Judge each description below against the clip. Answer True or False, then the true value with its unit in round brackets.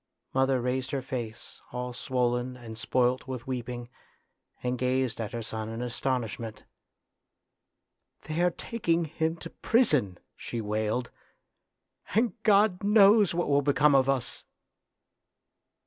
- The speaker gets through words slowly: True (130 wpm)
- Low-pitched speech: True (130 Hz)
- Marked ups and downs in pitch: False (4.7 semitones)